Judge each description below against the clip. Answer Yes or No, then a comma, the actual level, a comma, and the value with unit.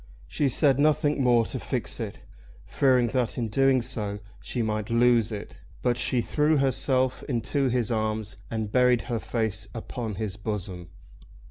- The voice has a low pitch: Yes, low, 120 Hz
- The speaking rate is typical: Yes, average, 155 wpm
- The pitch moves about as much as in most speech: Yes, average, 3.1 semitones